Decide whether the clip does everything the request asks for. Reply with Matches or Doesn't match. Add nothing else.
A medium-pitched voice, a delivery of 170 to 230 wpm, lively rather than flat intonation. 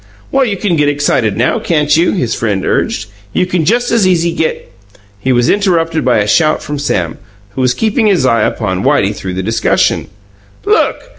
Matches